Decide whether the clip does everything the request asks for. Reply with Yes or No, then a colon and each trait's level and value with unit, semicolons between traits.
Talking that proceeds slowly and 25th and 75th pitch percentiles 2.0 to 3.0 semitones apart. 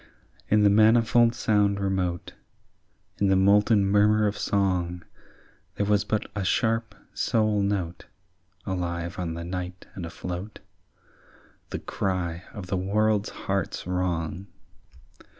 Yes: slow, 120 wpm; narrow, 2.6 semitones